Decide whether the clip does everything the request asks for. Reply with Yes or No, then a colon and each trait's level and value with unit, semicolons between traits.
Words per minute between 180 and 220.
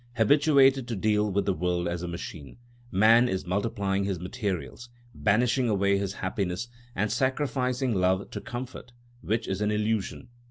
No: average, 155 wpm